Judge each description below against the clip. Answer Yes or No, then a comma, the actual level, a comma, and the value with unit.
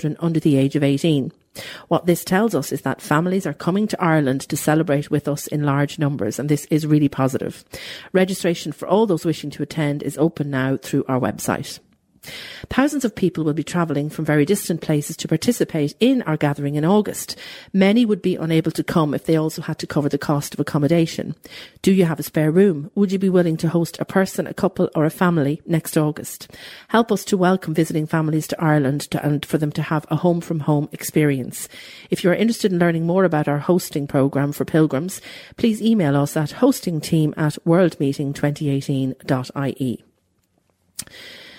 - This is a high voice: No, medium, 155 Hz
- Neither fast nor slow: Yes, average, 195 wpm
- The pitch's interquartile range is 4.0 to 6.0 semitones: No, average, 3.5 semitones